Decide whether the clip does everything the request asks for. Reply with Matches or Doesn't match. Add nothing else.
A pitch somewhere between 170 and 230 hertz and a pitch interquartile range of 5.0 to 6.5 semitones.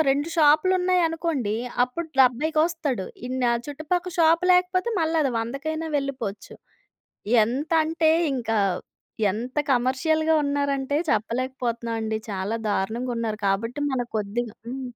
Doesn't match